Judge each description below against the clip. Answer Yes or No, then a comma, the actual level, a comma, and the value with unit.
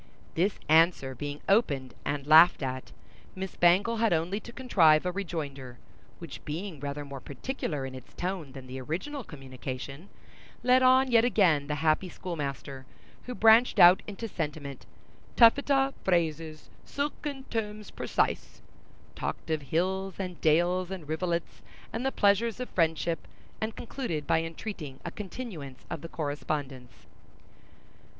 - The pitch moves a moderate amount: No, wide, 6.3 semitones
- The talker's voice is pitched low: No, medium, 170 Hz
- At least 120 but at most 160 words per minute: Yes, average, 140 wpm